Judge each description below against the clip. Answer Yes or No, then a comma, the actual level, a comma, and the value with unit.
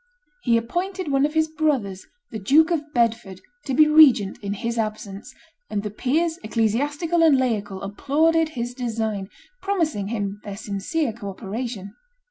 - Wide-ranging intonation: Yes, wide, 7.0 semitones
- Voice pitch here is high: Yes, high, 235 Hz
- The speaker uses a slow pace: No, average, 150 wpm